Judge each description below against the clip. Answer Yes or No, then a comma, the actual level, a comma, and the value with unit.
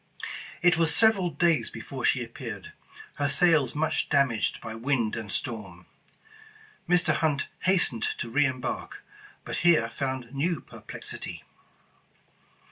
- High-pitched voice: No, medium, 140 Hz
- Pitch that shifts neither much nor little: No, wide, 6.1 semitones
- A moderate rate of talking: No, slow, 125 wpm